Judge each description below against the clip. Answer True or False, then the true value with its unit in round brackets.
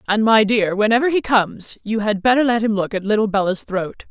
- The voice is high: True (215 Hz)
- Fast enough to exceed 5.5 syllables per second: True (5.7 syllables/s)